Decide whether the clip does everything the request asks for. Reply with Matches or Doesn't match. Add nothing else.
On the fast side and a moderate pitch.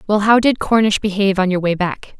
Doesn't match